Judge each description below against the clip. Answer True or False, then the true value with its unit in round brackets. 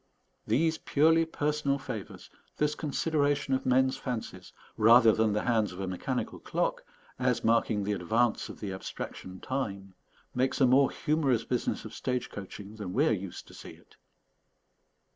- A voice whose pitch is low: True (125 Hz)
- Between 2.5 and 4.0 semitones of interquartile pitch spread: False (5.3 semitones)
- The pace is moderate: True (160 wpm)